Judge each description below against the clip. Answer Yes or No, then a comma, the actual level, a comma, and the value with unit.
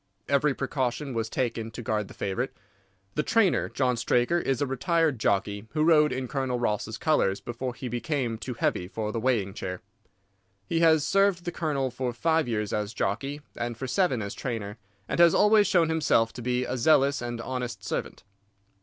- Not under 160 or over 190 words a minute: Yes, average, 185 wpm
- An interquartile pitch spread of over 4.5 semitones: Yes, average, 4.9 semitones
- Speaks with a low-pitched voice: Yes, low, 125 Hz